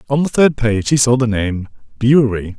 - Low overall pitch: Yes, low, 120 Hz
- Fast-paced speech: Yes, fast, 210 wpm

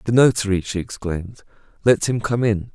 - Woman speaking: No, male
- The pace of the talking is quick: No, average, 175 wpm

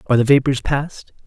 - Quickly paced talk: No, average, 190 wpm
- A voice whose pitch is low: Yes, low, 130 Hz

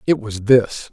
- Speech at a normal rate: Yes, average, 195 wpm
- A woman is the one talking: No, male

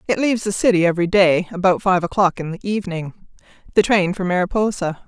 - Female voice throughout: Yes, female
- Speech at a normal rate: Yes, average, 190 wpm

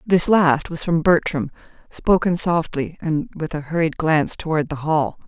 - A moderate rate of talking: Yes, average, 170 wpm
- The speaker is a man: No, female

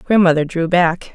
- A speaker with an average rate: Yes, average, 155 wpm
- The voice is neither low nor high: Yes, medium, 175 Hz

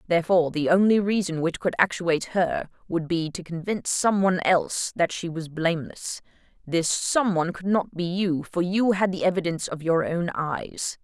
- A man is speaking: No, female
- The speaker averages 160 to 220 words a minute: Yes, average, 180 wpm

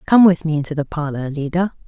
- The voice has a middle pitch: Yes, medium, 160 Hz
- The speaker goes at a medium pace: No, fast, 225 wpm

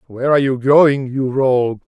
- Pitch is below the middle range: Yes, low, 130 Hz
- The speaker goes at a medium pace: Yes, average, 185 wpm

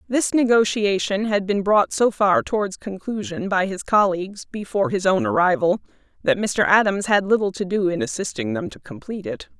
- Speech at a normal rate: Yes, average, 180 wpm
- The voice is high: Yes, high, 200 Hz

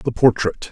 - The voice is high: No, low, 120 Hz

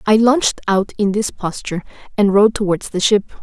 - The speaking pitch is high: Yes, high, 205 Hz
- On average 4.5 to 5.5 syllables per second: No, 6.0 syllables/s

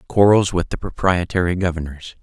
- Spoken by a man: Yes, male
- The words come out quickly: No, slow, 135 wpm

